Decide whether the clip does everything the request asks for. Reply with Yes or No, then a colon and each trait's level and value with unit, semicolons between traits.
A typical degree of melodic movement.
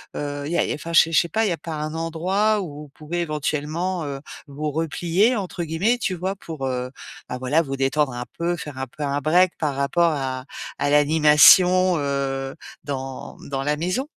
Yes: average, 3.7 semitones